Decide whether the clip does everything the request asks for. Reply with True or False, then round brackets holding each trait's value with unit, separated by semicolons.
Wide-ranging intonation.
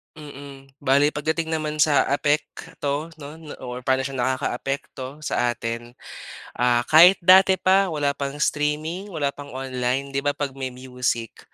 False (2.8 semitones)